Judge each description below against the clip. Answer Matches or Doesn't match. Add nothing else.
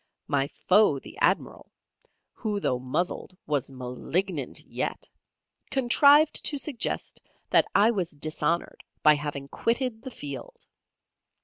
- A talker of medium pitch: Matches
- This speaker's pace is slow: Matches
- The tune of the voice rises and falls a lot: Matches